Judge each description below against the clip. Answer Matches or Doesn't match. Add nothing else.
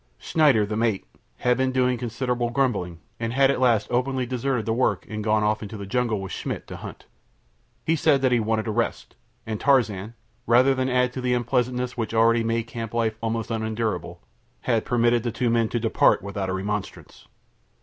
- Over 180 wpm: Matches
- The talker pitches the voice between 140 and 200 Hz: Doesn't match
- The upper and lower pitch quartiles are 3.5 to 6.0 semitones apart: Doesn't match